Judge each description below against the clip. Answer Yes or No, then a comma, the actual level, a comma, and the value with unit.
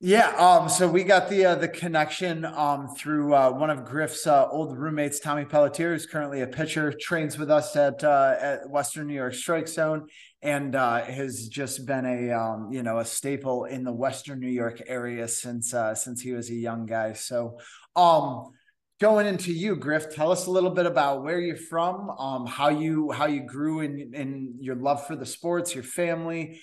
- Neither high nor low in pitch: Yes, medium, 145 Hz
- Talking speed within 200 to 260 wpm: Yes, fast, 205 wpm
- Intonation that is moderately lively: Yes, average, 4.2 semitones